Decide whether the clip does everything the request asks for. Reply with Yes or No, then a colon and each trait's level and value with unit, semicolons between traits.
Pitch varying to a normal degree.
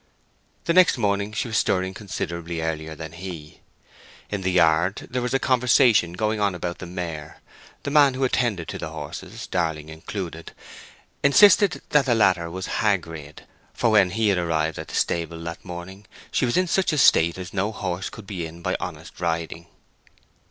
Yes: average, 4.9 semitones